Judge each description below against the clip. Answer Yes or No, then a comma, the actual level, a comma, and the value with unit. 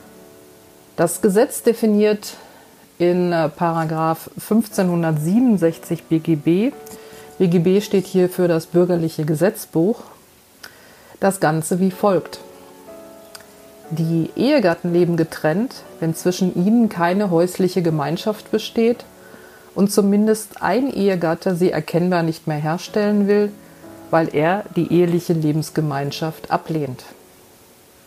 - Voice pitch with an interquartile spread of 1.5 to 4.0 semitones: Yes, average, 3.5 semitones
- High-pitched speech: No, medium, 175 Hz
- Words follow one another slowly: Yes, slow, 95 wpm